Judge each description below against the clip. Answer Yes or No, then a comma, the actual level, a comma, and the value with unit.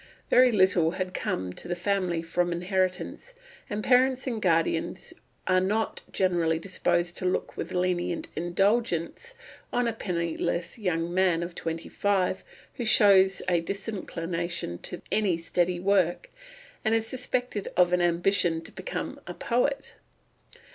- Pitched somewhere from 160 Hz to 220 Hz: Yes, medium, 185 Hz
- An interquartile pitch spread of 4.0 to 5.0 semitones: No, average, 3.4 semitones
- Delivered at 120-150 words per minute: Yes, average, 140 wpm